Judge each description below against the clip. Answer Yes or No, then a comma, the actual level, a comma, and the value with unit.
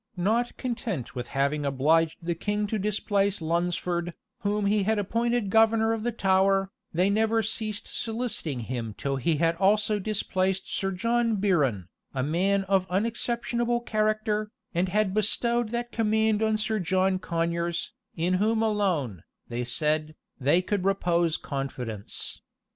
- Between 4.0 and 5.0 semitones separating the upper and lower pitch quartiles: Yes, average, 4.5 semitones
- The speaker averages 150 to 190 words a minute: No, average, 140 wpm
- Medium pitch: No, high, 195 Hz